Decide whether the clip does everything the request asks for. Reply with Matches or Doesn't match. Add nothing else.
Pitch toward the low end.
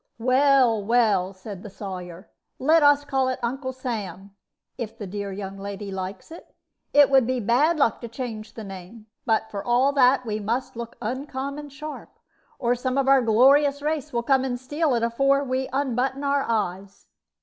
Doesn't match